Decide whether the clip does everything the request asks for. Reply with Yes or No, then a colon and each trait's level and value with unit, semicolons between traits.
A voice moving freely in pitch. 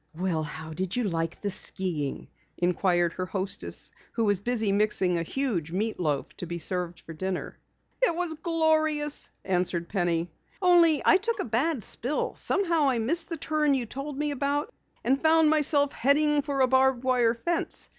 Yes: wide, 8.7 semitones